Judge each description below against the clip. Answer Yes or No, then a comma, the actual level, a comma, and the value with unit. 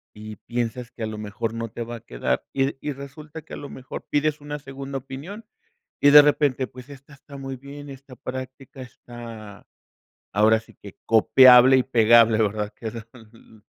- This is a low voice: Yes, low, 130 Hz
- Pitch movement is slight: No, average, 3.6 semitones